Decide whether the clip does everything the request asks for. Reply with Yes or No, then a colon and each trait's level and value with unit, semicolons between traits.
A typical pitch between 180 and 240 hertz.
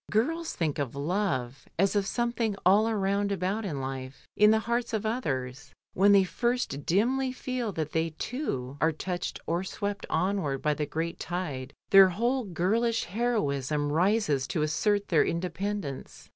Yes: high, 190 Hz